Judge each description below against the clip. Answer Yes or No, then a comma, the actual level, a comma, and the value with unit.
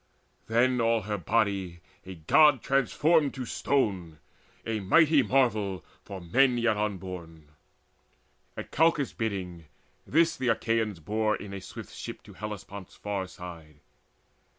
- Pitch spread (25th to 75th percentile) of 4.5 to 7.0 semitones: Yes, average, 5.2 semitones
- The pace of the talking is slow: Yes, slow, 130 wpm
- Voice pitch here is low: Yes, low, 105 Hz